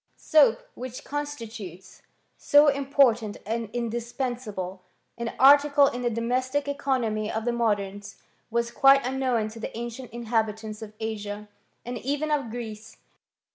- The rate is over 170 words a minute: No, slow, 135 wpm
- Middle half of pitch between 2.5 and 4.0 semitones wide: Yes, average, 3.5 semitones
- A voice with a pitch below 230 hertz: No, high, 235 Hz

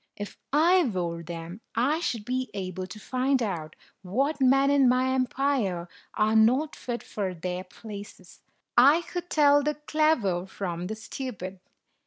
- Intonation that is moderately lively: No, wide, 6.9 semitones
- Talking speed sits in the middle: Yes, average, 150 wpm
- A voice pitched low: No, high, 235 Hz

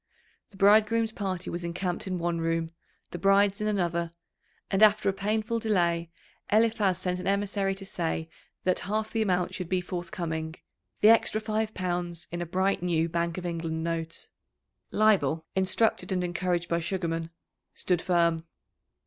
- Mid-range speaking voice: Yes, medium, 180 Hz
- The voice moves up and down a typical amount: Yes, average, 3.1 semitones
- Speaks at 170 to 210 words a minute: No, average, 155 wpm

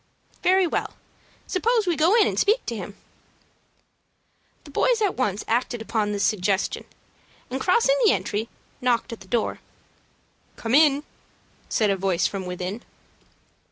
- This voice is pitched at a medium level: No, high, 240 Hz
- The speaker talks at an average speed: Yes, average, 145 wpm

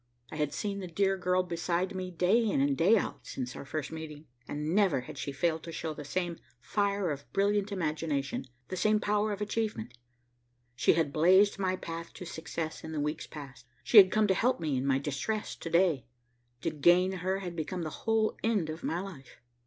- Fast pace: Yes, fast, 210 wpm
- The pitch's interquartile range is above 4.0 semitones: Yes, average, 4.5 semitones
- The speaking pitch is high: No, medium, 170 Hz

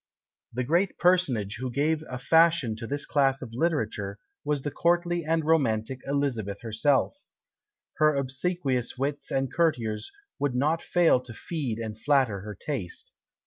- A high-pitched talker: No, low, 135 Hz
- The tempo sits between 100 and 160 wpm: Yes, average, 145 wpm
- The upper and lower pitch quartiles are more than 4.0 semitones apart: Yes, wide, 5.5 semitones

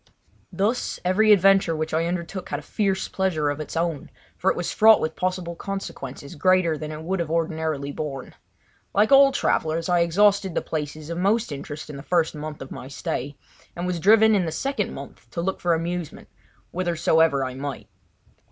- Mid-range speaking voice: Yes, medium, 170 Hz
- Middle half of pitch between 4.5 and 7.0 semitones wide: No, average, 3.7 semitones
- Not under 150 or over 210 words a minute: Yes, average, 190 wpm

